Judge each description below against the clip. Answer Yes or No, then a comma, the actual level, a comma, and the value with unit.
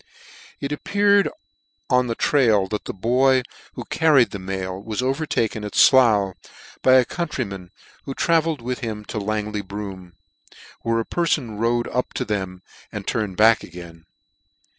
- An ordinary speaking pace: Yes, average, 155 wpm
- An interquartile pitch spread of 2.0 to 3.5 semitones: No, average, 4.7 semitones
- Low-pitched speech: Yes, low, 115 Hz